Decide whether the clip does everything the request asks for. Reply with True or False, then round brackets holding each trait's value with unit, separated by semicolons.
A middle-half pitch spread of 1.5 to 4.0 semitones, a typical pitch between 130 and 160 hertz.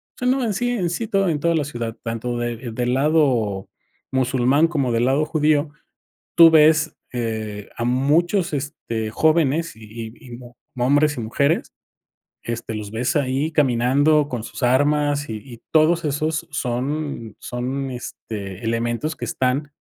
False (4.5 semitones; 135 Hz)